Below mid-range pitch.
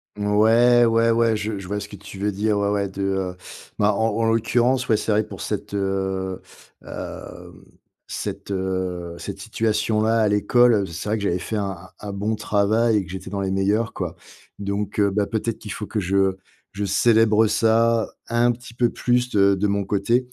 Yes: low, 105 Hz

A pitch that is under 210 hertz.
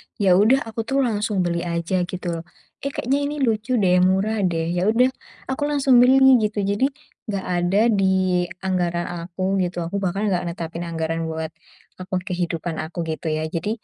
Yes: medium, 185 Hz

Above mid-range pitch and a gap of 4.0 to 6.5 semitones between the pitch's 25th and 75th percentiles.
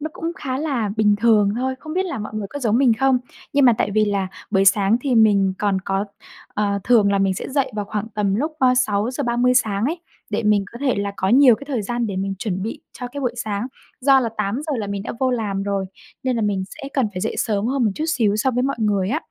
Yes: high, 220 Hz; average, 4.3 semitones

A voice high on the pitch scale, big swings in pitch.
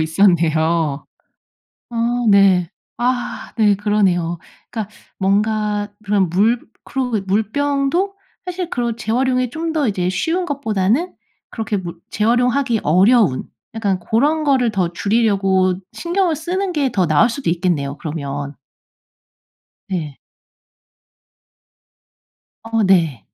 Yes: high, 210 Hz; wide, 5.7 semitones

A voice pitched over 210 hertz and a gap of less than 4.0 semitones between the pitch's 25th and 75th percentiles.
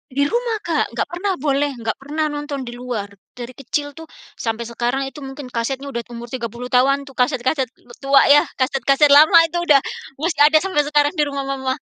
Yes: very high, 275 Hz; average, 2.9 semitones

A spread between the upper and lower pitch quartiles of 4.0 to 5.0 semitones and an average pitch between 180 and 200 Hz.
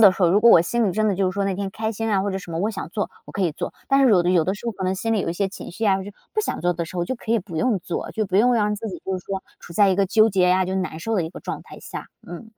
No: average, 3.2 semitones; high, 195 Hz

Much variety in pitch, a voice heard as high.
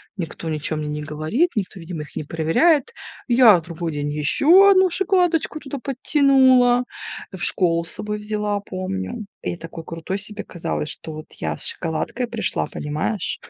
Yes: wide, 8.3 semitones; high, 195 Hz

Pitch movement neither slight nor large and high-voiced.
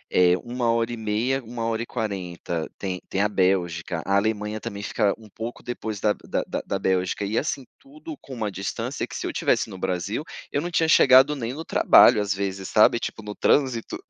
No: average, 3.8 semitones; low, 110 Hz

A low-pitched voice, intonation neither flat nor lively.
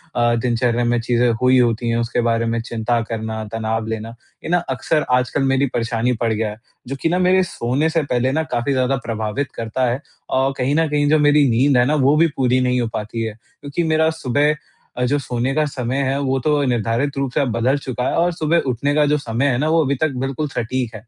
Yes: low, 125 Hz; average, 3.6 semitones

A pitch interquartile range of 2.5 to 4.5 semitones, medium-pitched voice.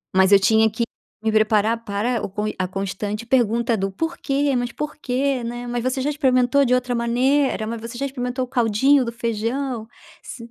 No: average, 2.9 semitones; high, 240 Hz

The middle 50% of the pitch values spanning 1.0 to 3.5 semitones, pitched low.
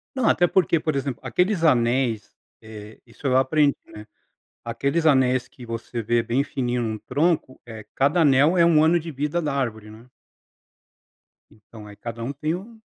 No: average, 5.1 semitones; low, 130 Hz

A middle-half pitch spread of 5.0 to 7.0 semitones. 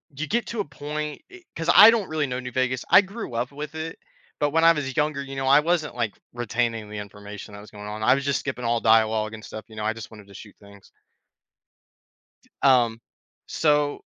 Yes: wide, 5.5 semitones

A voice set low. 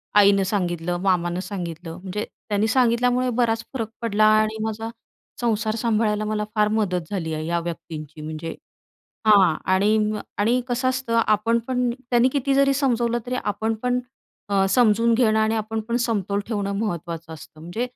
No: high, 215 Hz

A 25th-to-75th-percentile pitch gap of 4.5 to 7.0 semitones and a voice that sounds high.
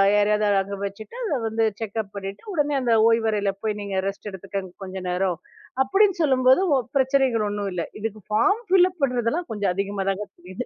Yes: average, 4.8 semitones; high, 210 Hz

